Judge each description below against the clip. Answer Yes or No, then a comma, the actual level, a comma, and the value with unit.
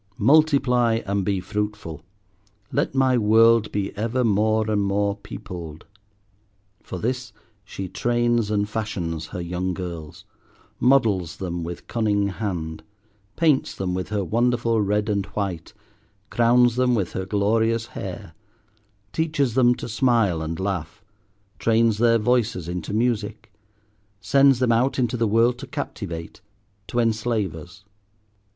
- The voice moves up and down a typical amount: Yes, average, 4.0 semitones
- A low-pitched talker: Yes, low, 110 Hz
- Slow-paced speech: Yes, slow, 130 wpm